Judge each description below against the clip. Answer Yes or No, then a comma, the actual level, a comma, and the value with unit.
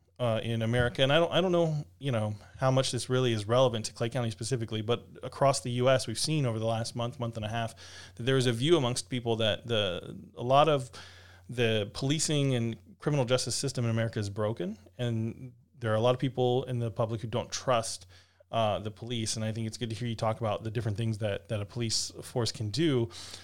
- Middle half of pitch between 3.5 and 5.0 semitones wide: No, narrow, 2.6 semitones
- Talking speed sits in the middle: No, fast, 240 wpm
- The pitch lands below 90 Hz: No, low, 115 Hz